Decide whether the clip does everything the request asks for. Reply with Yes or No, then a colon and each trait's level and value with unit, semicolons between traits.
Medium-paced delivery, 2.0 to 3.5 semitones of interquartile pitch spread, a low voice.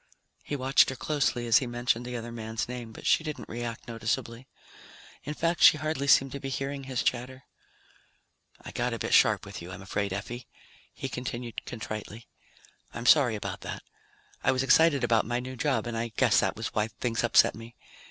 Yes: average, 195 wpm; average, 2.7 semitones; low, 120 Hz